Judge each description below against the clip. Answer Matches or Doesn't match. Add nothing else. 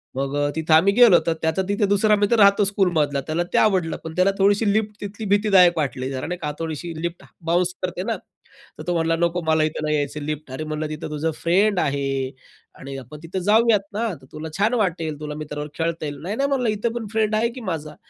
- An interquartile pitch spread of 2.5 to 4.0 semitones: Doesn't match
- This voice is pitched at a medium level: Matches